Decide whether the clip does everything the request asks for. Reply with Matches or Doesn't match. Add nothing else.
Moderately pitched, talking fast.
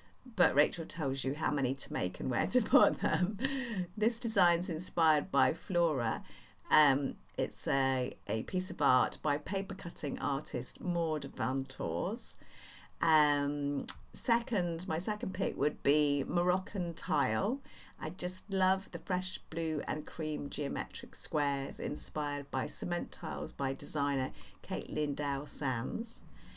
Doesn't match